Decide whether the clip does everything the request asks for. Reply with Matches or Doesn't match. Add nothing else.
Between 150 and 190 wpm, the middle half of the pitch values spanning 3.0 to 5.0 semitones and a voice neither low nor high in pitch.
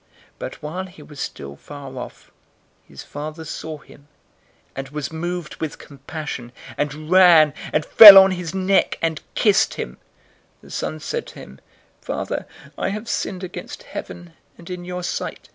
Matches